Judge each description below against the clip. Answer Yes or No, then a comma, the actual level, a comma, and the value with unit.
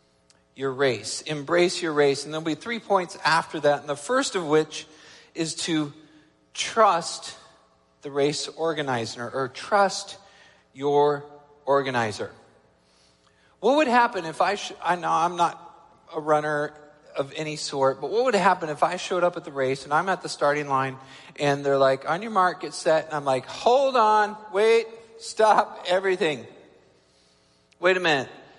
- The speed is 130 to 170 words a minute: Yes, average, 165 wpm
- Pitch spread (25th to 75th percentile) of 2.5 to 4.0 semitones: No, average, 5.1 semitones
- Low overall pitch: No, medium, 150 Hz